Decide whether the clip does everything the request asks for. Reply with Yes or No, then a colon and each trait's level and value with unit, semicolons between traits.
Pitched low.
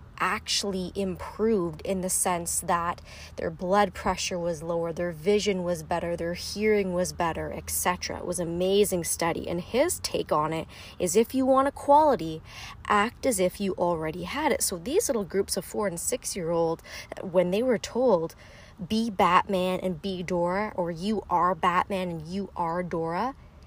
No: medium, 185 Hz